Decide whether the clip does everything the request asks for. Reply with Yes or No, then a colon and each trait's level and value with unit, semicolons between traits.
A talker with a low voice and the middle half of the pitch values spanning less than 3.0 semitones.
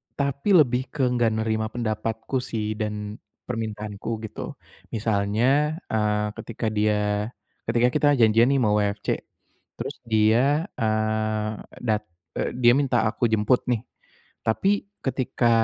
Yes: low, 110 Hz; narrow, 2.6 semitones